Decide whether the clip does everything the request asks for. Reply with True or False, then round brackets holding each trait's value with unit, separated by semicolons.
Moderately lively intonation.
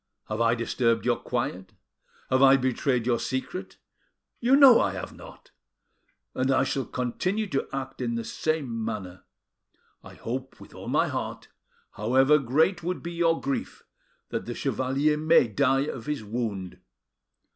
True (4.5 semitones)